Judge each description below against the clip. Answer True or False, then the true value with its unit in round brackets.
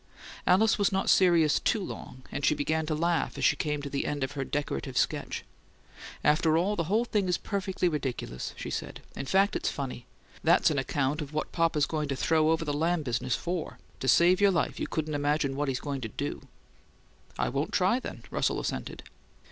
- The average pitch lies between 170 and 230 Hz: False (155 Hz)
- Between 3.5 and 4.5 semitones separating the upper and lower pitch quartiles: True (3.9 semitones)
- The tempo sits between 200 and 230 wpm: True (205 wpm)